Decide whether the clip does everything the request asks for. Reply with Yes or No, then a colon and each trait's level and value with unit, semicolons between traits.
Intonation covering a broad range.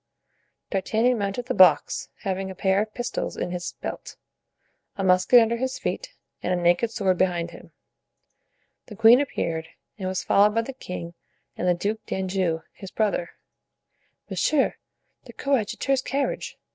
No: average, 4.4 semitones